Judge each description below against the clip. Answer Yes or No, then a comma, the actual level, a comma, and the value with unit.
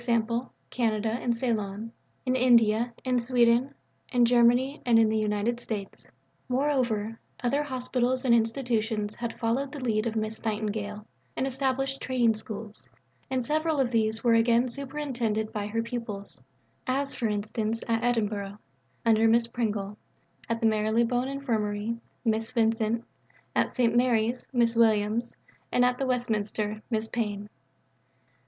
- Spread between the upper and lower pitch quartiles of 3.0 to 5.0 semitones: No, narrow, 2.4 semitones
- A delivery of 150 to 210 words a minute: No, average, 140 wpm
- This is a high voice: Yes, high, 230 Hz